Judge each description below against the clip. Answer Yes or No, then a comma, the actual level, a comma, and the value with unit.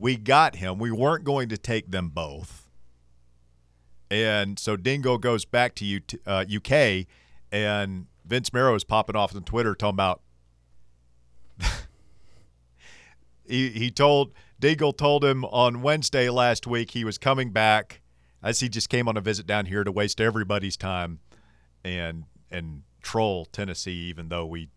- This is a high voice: No, low, 105 Hz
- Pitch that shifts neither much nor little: No, wide, 6.6 semitones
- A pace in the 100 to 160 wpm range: Yes, average, 150 wpm